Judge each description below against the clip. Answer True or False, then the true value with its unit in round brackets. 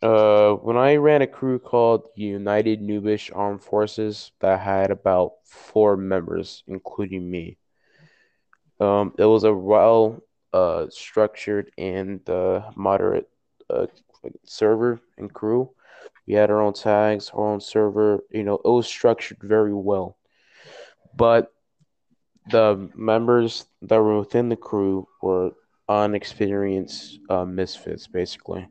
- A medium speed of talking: False (125 wpm)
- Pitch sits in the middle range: False (105 Hz)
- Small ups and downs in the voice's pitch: True (2.2 semitones)